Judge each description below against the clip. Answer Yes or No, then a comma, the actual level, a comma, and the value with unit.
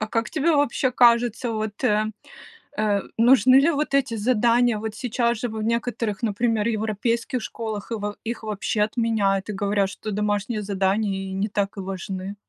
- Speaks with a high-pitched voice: Yes, high, 215 Hz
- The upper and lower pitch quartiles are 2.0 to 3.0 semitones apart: Yes, narrow, 2.4 semitones